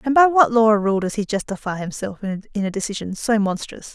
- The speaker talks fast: Yes, fast, 230 wpm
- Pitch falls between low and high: No, high, 210 Hz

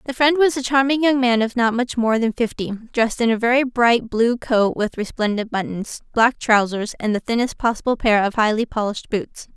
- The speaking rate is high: Yes, fast, 215 wpm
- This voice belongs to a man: No, female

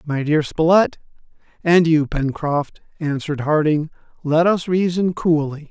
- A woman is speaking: No, male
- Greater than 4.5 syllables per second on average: No, 4.2 syllables/s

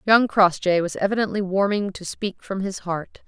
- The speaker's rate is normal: Yes, average, 185 wpm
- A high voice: Yes, high, 195 Hz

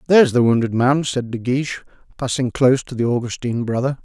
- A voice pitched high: No, low, 125 Hz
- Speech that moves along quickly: Yes, fast, 210 wpm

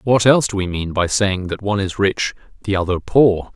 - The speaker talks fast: Yes, fast, 235 wpm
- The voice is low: Yes, low, 100 Hz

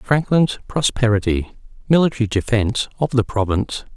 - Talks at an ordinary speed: No, slow, 105 wpm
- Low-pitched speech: Yes, low, 120 Hz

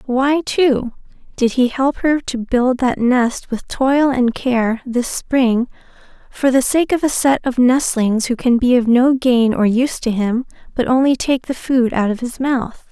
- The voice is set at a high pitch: Yes, very high, 250 Hz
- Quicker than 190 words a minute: Yes, average, 200 wpm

